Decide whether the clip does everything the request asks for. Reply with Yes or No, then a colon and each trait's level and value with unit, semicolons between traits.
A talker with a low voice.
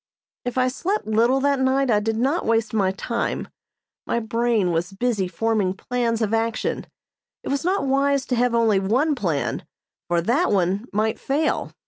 No: high, 230 Hz